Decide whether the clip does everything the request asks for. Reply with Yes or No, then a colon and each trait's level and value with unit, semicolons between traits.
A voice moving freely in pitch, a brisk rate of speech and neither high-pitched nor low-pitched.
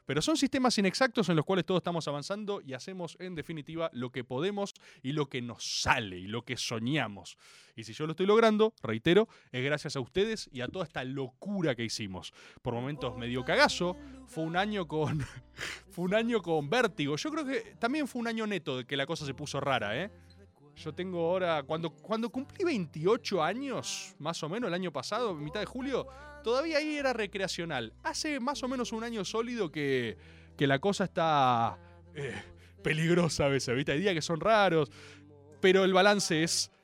Yes: wide, 7.6 semitones; fast, 195 wpm; medium, 165 Hz